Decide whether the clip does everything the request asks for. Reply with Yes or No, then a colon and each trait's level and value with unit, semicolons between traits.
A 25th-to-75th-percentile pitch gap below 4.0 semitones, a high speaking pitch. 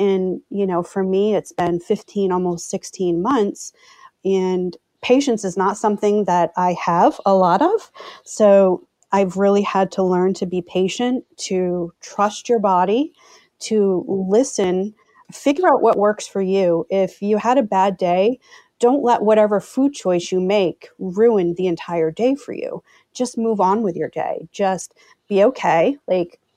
Yes: average, 3.5 semitones; high, 195 Hz